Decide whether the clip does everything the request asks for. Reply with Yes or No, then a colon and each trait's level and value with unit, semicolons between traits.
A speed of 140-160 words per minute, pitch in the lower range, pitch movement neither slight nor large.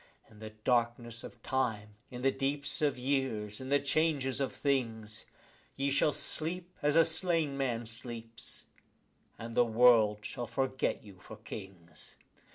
Yes: average, 155 wpm; low, 125 Hz; average, 3.9 semitones